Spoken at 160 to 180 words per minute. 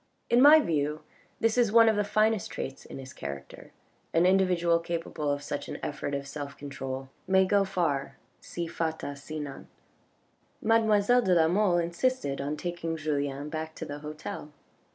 Yes: average, 165 wpm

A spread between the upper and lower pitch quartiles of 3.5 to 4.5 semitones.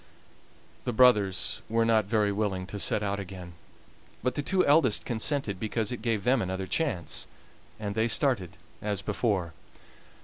Yes: average, 3.8 semitones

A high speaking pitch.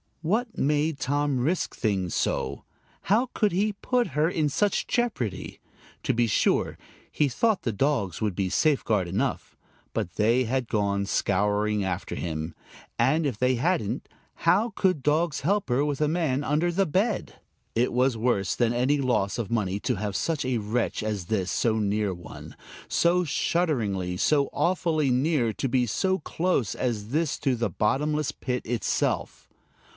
No: low, 130 Hz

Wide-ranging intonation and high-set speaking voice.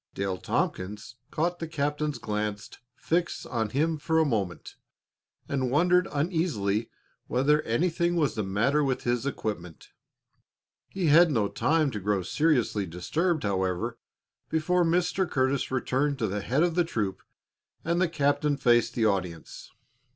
No: wide, 7.3 semitones; low, 135 Hz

